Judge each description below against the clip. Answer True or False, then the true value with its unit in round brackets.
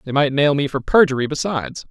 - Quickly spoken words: True (220 wpm)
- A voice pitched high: False (140 Hz)